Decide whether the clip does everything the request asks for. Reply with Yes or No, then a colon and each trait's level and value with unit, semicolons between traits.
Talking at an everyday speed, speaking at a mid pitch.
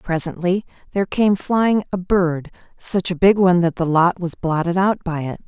Yes: average, 185 wpm; medium, 180 Hz